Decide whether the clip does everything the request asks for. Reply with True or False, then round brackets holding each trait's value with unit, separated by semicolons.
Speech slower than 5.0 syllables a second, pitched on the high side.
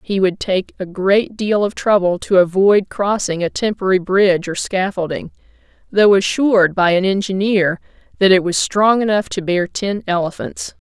True (4.8 syllables/s; 195 Hz)